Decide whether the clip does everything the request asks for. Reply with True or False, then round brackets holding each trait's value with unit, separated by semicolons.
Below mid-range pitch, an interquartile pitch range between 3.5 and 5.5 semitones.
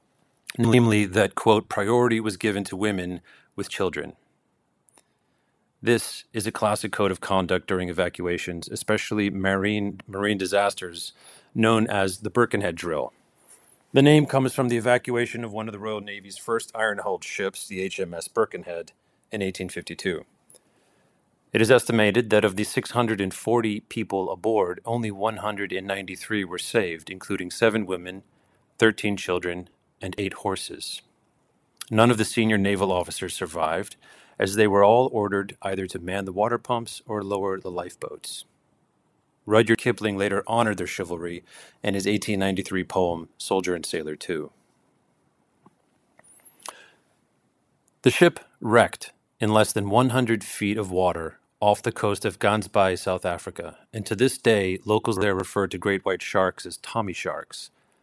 False (105 Hz; 2.8 semitones)